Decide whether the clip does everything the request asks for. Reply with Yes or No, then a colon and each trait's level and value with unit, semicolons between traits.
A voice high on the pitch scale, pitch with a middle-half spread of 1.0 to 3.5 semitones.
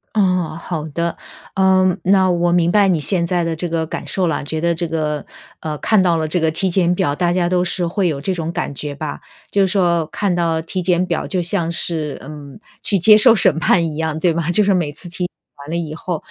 No: medium, 170 Hz; narrow, 2.4 semitones